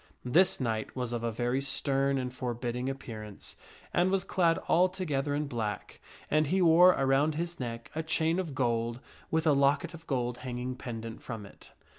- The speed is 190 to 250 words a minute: No, average, 170 wpm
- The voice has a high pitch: No, low, 135 Hz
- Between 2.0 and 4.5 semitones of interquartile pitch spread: No, average, 5.0 semitones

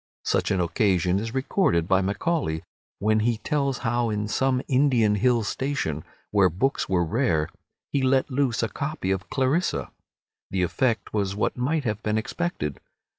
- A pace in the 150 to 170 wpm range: Yes, average, 160 wpm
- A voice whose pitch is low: Yes, low, 110 Hz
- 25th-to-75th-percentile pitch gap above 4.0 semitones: Yes, wide, 5.5 semitones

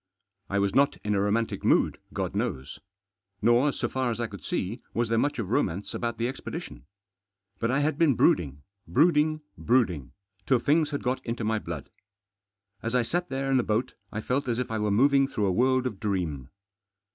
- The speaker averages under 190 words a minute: No, average, 200 wpm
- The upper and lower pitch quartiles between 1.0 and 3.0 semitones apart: No, average, 4.6 semitones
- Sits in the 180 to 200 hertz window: No, low, 115 Hz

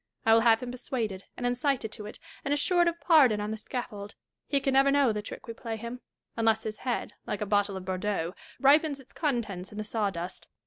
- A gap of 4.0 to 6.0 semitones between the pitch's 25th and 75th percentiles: Yes, average, 4.4 semitones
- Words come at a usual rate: No, fast, 220 wpm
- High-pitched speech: Yes, high, 225 Hz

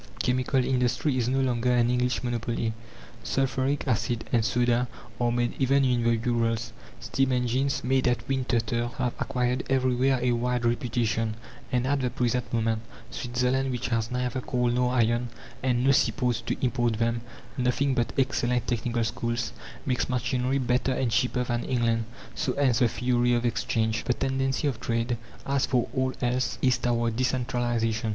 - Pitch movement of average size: No, narrow, 1.5 semitones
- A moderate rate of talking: Yes, average, 165 wpm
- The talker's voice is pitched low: Yes, low, 125 Hz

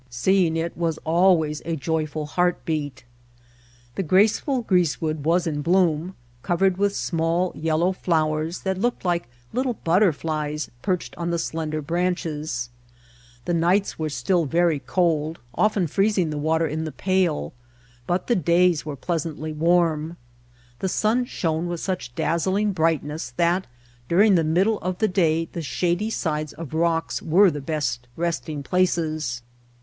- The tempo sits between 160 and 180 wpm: No, average, 150 wpm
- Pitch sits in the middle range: Yes, medium, 165 Hz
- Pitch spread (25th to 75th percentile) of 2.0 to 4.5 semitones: Yes, average, 2.9 semitones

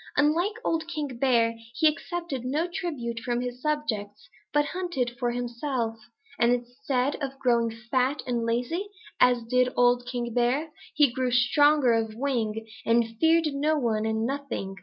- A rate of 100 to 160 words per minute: Yes, average, 155 wpm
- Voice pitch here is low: No, very high, 250 Hz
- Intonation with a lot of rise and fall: No, average, 3.8 semitones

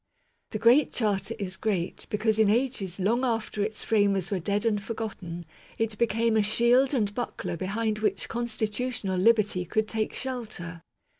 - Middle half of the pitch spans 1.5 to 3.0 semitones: Yes, narrow, 2.6 semitones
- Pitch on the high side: Yes, high, 215 Hz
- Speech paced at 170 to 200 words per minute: No, average, 155 wpm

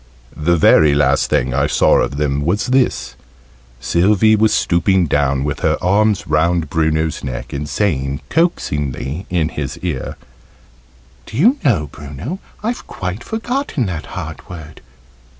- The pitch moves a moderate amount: No, wide, 6.5 semitones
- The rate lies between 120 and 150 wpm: Yes, average, 140 wpm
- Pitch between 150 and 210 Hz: No, very low, 80 Hz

